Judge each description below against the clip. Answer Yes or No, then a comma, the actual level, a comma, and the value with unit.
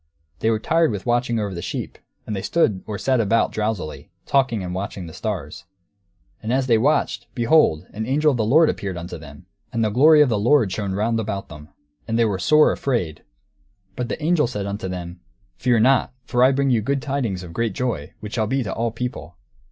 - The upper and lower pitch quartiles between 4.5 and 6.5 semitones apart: Yes, average, 4.9 semitones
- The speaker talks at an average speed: No, fast, 220 wpm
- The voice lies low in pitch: Yes, low, 110 Hz